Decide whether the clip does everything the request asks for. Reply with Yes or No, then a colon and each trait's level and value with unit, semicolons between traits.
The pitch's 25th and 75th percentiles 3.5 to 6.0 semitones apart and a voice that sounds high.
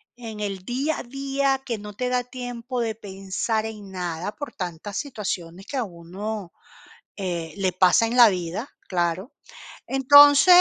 Yes: average, 5.2 semitones; high, 215 Hz